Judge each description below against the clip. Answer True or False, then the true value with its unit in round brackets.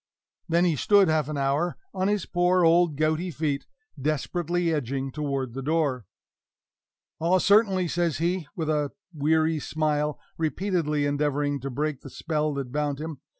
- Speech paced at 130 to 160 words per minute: True (150 wpm)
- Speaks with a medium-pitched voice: True (155 Hz)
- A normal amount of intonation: True (3.2 semitones)